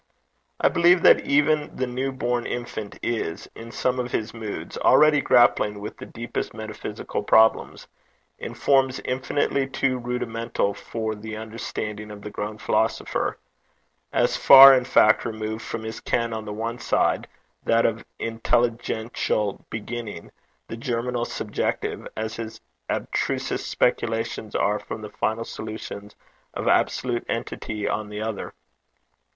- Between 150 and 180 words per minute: No, slow, 135 wpm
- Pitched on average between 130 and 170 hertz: No, low, 115 Hz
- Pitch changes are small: Yes, narrow, 2.2 semitones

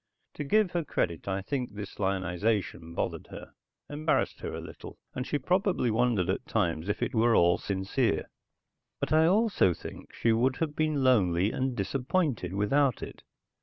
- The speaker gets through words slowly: No, average, 165 wpm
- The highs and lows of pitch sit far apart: Yes, wide, 7.3 semitones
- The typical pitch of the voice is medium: No, low, 115 Hz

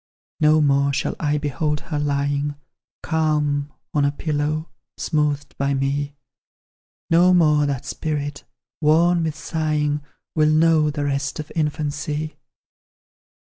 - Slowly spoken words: Yes, slow, 120 wpm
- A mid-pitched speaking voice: Yes, medium, 150 Hz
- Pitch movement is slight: Yes, narrow, 1.4 semitones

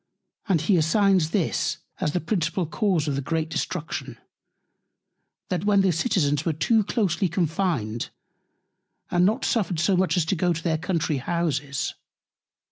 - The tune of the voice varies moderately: Yes, average, 3.4 semitones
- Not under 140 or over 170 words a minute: Yes, average, 145 wpm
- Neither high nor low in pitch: Yes, medium, 170 Hz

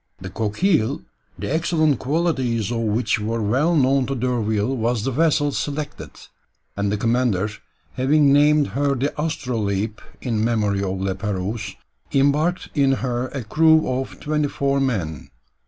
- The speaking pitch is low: Yes, low, 125 Hz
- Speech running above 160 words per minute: No, average, 145 wpm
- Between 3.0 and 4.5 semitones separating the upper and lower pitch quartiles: No, average, 5.1 semitones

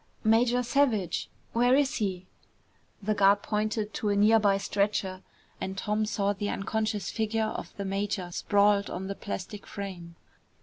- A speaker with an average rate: Yes, average, 150 wpm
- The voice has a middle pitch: No, high, 205 Hz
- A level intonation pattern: Yes, narrow, 1.9 semitones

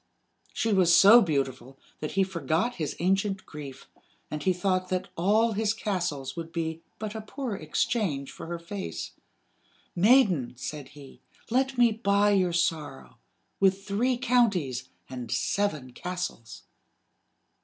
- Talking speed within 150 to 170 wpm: No, slow, 135 wpm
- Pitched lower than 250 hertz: Yes, medium, 185 Hz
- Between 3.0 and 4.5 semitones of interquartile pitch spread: No, average, 5.3 semitones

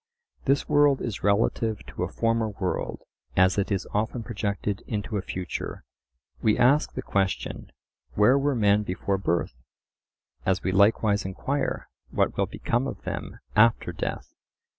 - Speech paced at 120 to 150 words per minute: Yes, average, 145 wpm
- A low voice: Yes, low, 105 Hz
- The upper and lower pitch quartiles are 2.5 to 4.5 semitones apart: Yes, average, 3.0 semitones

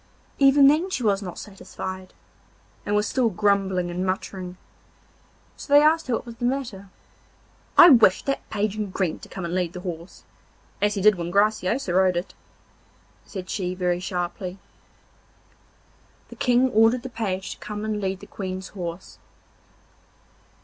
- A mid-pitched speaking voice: No, high, 200 Hz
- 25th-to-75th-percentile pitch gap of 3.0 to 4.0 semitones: Yes, average, 3.7 semitones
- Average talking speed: Yes, average, 165 wpm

